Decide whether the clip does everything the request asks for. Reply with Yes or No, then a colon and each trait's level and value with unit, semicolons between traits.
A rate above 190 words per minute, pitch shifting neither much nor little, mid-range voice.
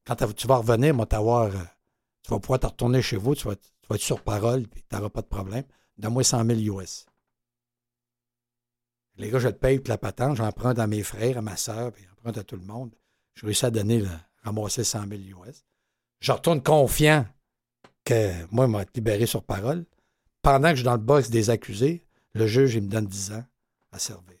No: average, 210 wpm; average, 3.4 semitones; low, 115 Hz